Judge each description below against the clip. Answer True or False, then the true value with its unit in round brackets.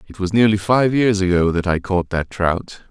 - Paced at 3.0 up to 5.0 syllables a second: True (4.8 syllables/s)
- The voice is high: False (95 Hz)